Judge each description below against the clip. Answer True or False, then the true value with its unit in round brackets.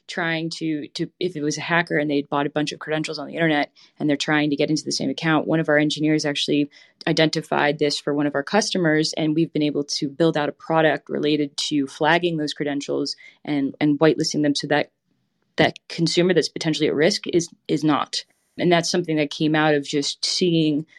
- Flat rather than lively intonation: True (1.8 semitones)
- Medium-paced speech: False (220 wpm)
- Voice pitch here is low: False (155 Hz)